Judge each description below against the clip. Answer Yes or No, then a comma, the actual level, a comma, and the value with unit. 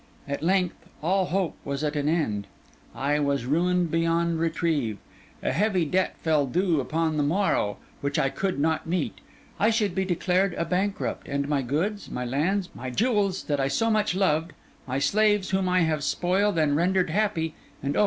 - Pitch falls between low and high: Yes, medium, 165 Hz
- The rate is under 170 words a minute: No, average, 185 wpm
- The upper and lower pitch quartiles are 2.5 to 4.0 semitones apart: No, average, 4.8 semitones